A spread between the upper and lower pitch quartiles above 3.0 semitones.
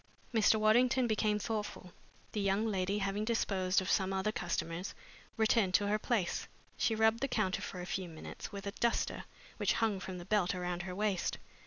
No: average, 2.7 semitones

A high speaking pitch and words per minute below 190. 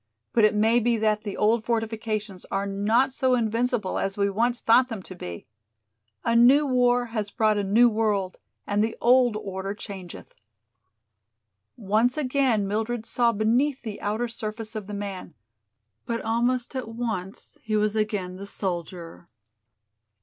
Yes: high, 220 Hz; average, 155 wpm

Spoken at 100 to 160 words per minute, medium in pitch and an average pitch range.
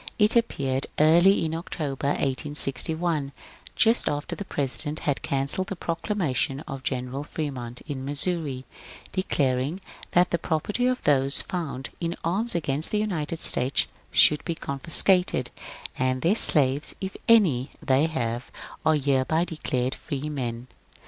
Yes: slow, 135 wpm; medium, 150 Hz; average, 4.3 semitones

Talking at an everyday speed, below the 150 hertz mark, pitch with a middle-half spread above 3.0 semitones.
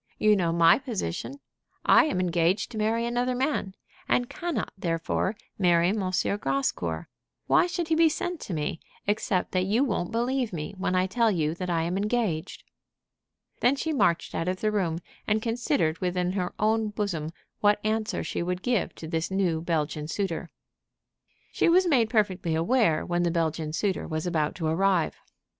No: average, 175 wpm; high, 190 Hz; average, 5.1 semitones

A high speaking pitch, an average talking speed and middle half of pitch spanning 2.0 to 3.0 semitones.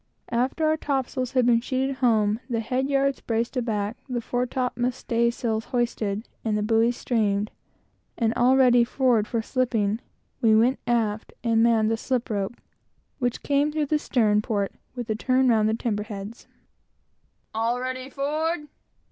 Yes: high, 235 Hz; average, 165 wpm; average, 2.7 semitones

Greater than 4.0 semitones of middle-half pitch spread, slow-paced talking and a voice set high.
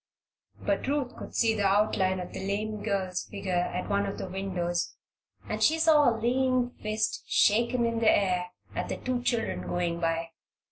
No: average, 4.4 semitones; average, 180 wpm; high, 205 Hz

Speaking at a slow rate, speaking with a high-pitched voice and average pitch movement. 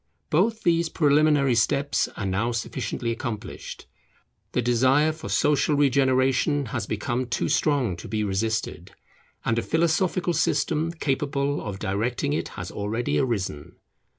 No: slow, 130 wpm; low, 130 Hz; average, 4.8 semitones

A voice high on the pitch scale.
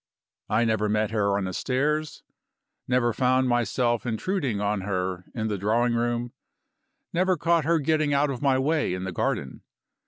No: low, 120 Hz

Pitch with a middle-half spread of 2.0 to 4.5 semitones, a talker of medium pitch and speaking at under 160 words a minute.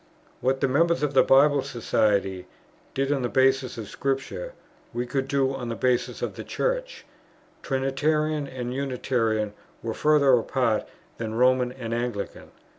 No: average, 2.7 semitones; low, 130 Hz; average, 150 wpm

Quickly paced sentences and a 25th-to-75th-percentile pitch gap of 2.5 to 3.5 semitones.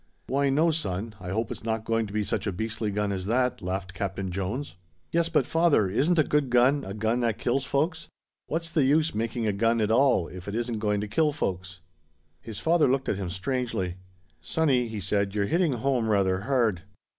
No: fast, 210 wpm; wide, 5.5 semitones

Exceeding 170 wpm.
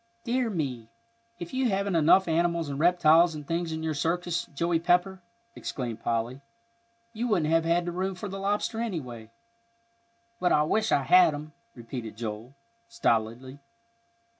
No: average, 150 wpm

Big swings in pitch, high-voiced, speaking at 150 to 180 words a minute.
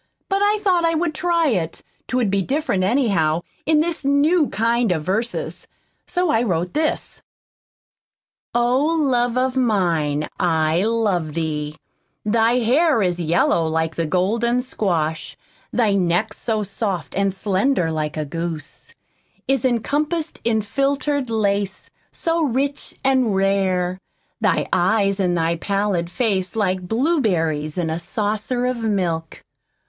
No: wide, 6.8 semitones; high, 210 Hz; slow, 135 wpm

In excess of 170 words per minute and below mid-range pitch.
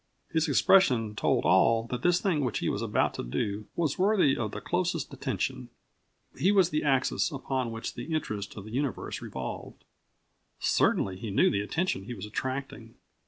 Yes: average, 180 wpm; low, 130 Hz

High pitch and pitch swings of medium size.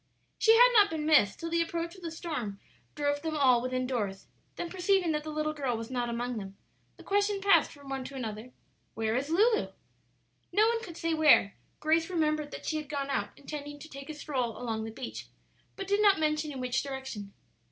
Yes: very high, 295 Hz; average, 5.0 semitones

